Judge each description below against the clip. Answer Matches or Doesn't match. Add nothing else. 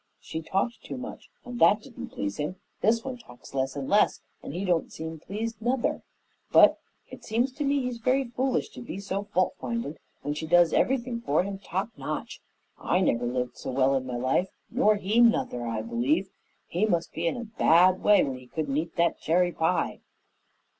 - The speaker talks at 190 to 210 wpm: Matches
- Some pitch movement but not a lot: Doesn't match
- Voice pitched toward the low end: Doesn't match